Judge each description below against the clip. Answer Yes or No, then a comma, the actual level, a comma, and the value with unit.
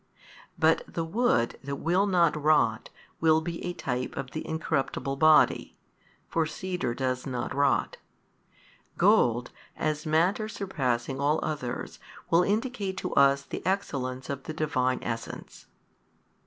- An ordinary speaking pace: No, slow, 130 wpm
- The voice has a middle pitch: Yes, medium, 155 Hz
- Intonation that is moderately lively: Yes, average, 4.6 semitones